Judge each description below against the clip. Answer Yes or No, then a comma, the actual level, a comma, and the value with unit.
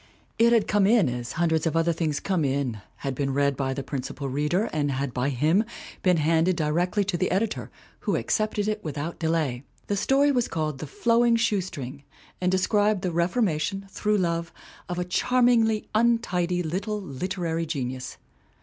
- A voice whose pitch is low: No, medium, 170 Hz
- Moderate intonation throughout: No, wide, 6.1 semitones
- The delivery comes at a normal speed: Yes, average, 175 wpm